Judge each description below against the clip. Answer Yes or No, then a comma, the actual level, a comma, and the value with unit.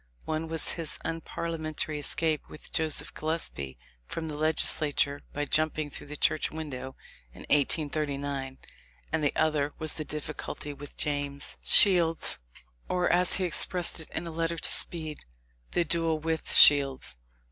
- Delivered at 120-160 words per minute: Yes, average, 150 wpm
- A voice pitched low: No, medium, 155 Hz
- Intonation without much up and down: Yes, narrow, 2.1 semitones